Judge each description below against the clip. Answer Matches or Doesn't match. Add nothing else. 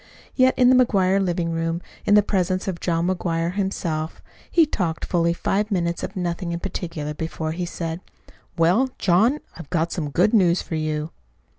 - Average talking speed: Matches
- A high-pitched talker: Doesn't match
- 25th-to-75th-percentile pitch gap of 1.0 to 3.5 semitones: Matches